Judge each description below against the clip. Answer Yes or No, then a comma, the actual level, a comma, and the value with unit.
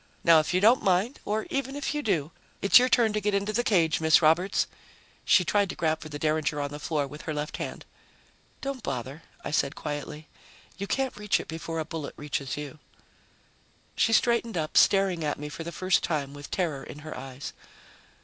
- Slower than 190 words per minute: No, fast, 205 wpm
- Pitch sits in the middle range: Yes, medium, 165 Hz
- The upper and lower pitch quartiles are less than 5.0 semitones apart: No, wide, 5.6 semitones